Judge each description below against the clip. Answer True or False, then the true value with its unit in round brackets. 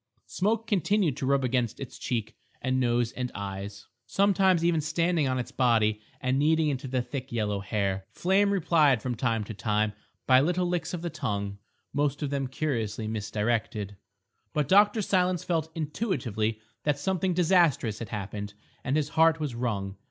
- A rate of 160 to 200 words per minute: True (165 wpm)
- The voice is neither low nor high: False (130 Hz)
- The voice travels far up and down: True (7.2 semitones)